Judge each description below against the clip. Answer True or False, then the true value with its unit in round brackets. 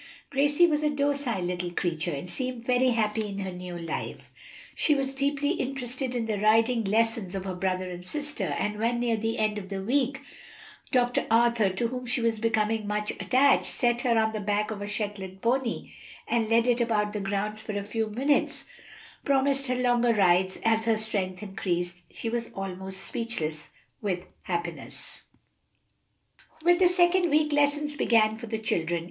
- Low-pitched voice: False (225 Hz)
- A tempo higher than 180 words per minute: False (175 wpm)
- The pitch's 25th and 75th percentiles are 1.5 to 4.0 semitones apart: False (4.5 semitones)